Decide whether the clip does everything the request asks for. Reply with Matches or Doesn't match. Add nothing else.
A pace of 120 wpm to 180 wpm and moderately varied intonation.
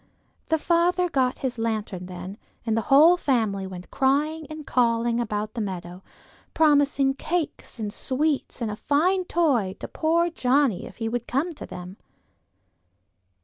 Doesn't match